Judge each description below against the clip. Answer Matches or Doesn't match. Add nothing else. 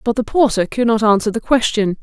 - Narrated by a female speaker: Matches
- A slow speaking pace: Doesn't match